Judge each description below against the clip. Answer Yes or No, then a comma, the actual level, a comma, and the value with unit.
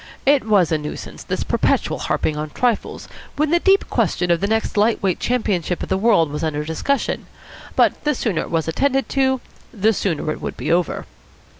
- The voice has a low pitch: No, high, 200 Hz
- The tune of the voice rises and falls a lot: Yes, wide, 7.5 semitones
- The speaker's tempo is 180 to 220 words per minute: Yes, average, 190 wpm